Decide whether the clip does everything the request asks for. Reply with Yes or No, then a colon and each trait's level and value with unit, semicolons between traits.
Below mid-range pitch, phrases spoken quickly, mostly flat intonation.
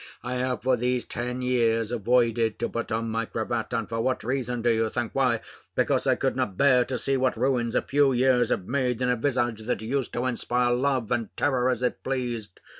Yes: low, 125 Hz; fast, 220 wpm; narrow, 1.9 semitones